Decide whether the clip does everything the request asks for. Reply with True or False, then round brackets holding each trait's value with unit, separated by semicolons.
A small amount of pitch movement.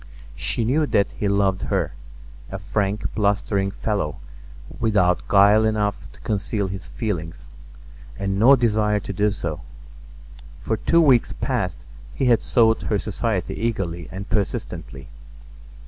True (2.3 semitones)